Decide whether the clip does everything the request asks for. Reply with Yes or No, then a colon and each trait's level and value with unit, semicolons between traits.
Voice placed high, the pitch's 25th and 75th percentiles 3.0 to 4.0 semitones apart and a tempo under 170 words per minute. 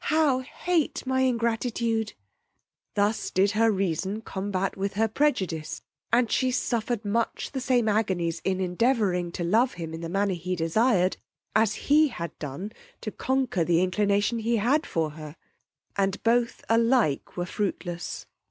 No: high, 210 Hz; average, 4.7 semitones; average, 150 wpm